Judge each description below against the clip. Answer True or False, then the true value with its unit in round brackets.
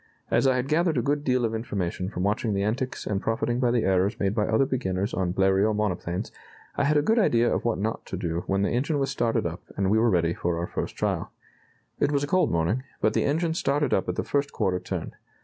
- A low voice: True (110 Hz)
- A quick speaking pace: True (250 wpm)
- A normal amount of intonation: False (6.0 semitones)